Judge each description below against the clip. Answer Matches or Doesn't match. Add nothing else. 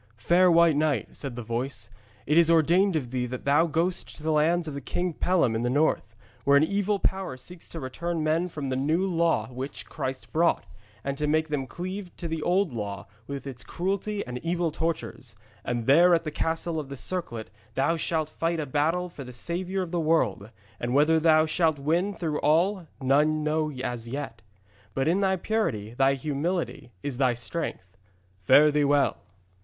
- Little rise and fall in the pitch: Doesn't match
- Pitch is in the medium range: Matches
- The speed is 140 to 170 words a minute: Doesn't match